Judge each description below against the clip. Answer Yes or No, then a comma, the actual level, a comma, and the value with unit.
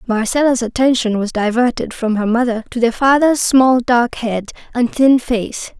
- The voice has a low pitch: No, high, 240 Hz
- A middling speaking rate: Yes, average, 165 wpm